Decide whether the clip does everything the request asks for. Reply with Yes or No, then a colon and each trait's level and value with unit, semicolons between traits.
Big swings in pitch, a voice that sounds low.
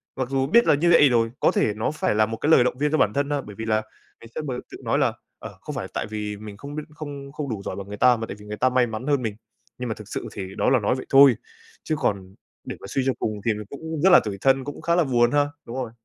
No: average, 4.9 semitones; low, 125 Hz